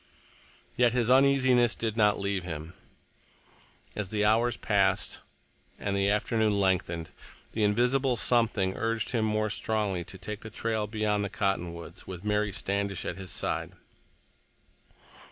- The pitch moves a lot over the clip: No, average, 2.7 semitones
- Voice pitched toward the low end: Yes, low, 105 Hz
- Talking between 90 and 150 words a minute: Yes, slow, 135 wpm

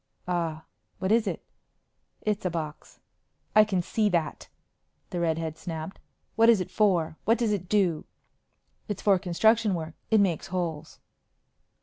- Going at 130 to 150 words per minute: Yes, average, 145 wpm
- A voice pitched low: No, medium, 180 Hz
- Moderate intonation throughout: Yes, average, 4.3 semitones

